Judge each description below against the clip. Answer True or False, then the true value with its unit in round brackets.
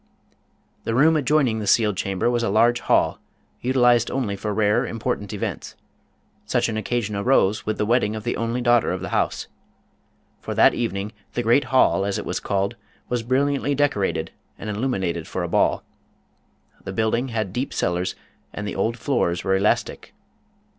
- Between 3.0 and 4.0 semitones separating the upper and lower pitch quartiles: True (3.4 semitones)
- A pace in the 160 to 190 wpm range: True (175 wpm)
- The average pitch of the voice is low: True (110 Hz)